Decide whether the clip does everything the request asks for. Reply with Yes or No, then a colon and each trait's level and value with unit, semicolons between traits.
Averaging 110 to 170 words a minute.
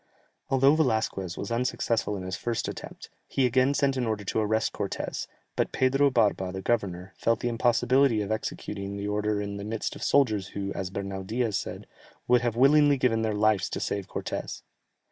No: average, 185 wpm